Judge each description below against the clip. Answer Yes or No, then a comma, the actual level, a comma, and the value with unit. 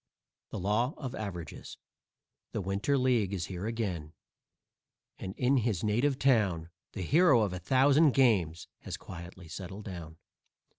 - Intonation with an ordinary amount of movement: No, wide, 6.1 semitones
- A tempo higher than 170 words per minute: No, average, 140 wpm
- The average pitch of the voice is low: Yes, low, 105 Hz